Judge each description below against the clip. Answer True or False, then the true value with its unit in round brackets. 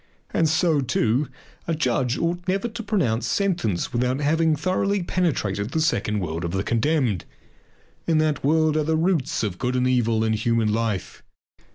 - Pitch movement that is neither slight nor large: False (6.4 semitones)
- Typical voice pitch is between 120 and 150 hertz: True (140 Hz)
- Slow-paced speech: False (175 wpm)